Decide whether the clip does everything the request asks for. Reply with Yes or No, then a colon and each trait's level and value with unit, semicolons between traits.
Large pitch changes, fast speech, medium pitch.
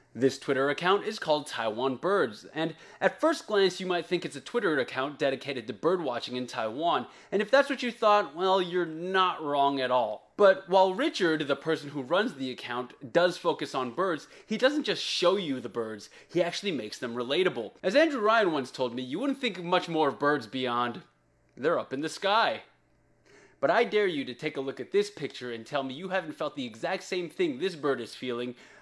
Yes: wide, 6.8 semitones; fast, 220 wpm; medium, 160 Hz